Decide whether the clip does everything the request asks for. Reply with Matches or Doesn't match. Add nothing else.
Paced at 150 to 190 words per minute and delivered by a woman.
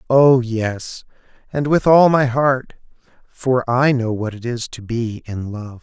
Doesn't match